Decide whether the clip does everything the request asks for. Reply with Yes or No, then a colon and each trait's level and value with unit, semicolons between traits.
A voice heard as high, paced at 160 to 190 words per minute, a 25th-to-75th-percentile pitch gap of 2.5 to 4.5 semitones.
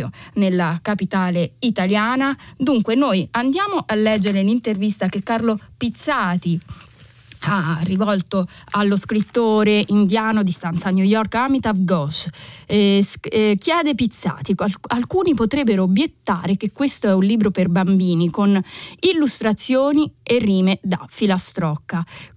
No: high, 205 Hz; average, 120 wpm; average, 3.7 semitones